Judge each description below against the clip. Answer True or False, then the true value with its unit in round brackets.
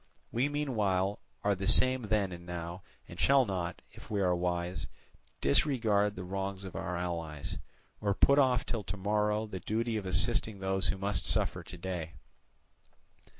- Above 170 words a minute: False (165 wpm)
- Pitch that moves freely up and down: False (3.3 semitones)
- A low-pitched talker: True (100 Hz)